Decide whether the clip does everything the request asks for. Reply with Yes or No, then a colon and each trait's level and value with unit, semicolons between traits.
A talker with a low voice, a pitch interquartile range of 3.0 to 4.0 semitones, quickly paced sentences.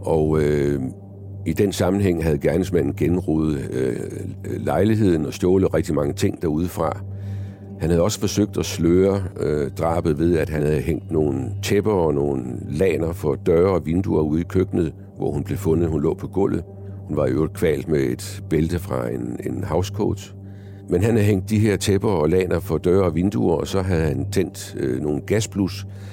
No: very low, 95 Hz; average, 3.7 semitones; average, 185 wpm